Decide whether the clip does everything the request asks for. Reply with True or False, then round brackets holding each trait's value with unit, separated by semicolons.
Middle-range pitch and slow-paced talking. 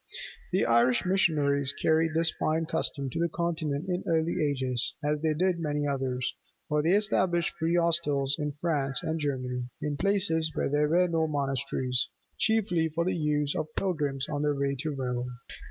False (150 Hz; 170 wpm)